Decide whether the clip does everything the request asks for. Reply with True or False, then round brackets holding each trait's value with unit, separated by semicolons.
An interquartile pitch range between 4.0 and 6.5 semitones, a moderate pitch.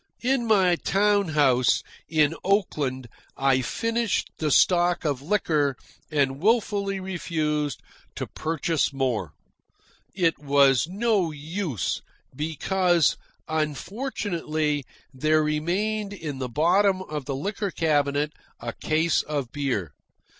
True (5.1 semitones; 155 Hz)